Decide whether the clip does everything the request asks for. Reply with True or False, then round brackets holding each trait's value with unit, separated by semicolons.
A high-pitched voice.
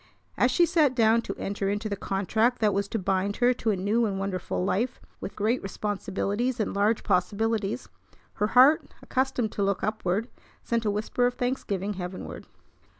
True (210 Hz)